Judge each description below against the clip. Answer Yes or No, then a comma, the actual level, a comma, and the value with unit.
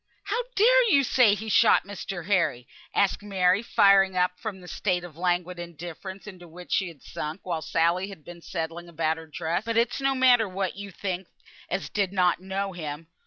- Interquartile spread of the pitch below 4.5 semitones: Yes, average, 2.9 semitones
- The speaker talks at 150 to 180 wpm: No, average, 195 wpm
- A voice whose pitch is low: No, medium, 185 Hz